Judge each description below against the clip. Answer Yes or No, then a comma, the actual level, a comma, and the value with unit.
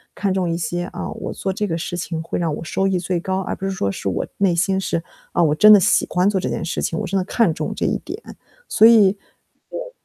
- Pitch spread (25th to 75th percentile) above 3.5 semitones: No, narrow, 2.5 semitones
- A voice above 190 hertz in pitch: No, medium, 185 Hz